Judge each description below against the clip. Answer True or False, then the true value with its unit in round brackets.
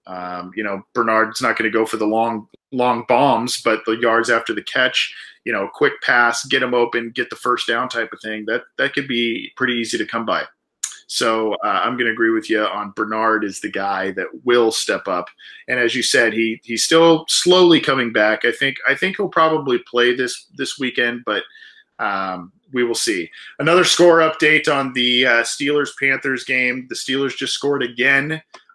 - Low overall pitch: True (120 Hz)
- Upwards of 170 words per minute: True (205 wpm)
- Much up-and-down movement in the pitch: False (3.5 semitones)